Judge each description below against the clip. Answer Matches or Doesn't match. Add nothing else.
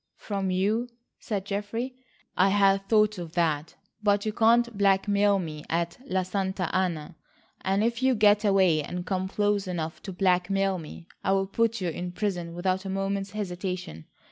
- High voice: Matches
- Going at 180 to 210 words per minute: Doesn't match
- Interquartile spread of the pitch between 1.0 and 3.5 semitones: Matches